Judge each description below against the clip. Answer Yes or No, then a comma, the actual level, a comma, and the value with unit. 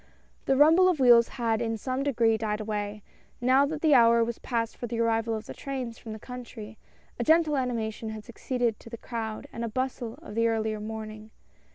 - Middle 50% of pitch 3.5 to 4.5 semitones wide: No, narrow, 2.6 semitones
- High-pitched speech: Yes, high, 230 Hz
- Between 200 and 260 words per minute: Yes, fast, 205 wpm